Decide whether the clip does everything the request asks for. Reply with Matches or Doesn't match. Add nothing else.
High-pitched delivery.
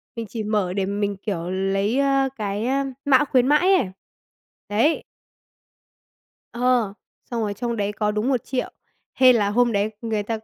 Matches